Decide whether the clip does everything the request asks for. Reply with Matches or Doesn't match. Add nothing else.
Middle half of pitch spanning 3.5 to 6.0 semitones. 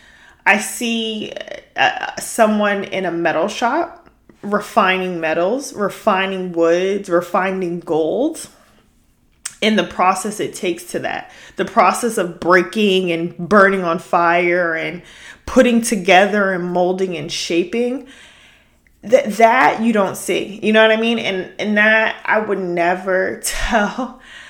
Matches